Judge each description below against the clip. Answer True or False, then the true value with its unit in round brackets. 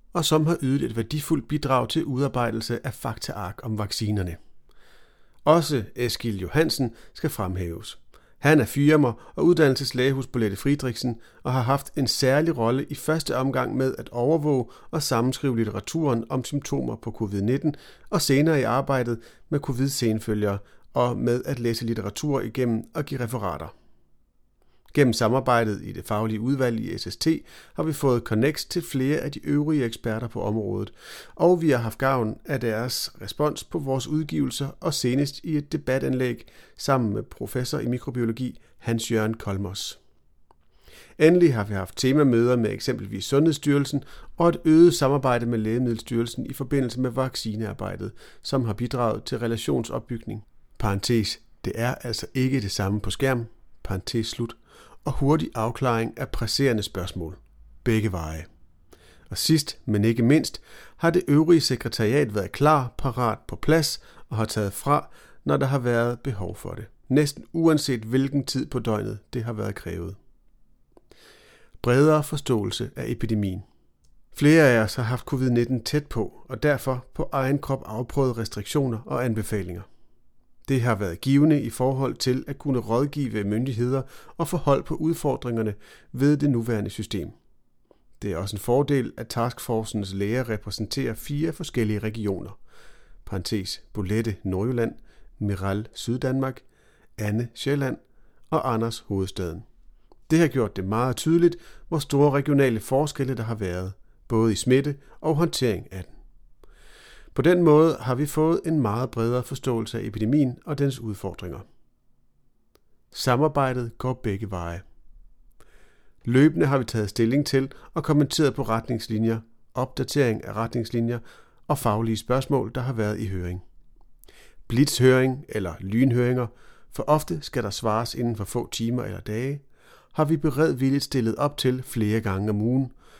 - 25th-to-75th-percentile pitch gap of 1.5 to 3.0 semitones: False (4.2 semitones)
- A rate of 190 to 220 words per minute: False (150 wpm)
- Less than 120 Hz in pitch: False (125 Hz)